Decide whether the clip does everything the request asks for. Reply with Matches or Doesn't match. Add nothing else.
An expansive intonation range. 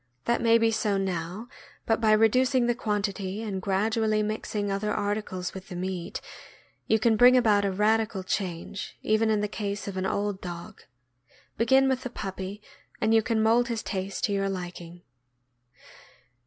Doesn't match